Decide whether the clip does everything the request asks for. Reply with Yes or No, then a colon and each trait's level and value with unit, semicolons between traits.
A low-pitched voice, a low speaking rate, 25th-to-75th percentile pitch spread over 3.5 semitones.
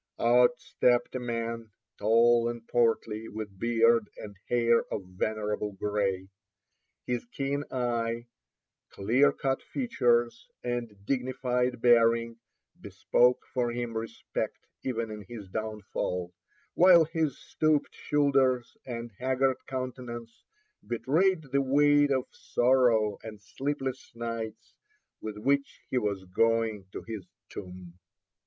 No: low, 120 Hz; slow, 115 wpm; average, 2.9 semitones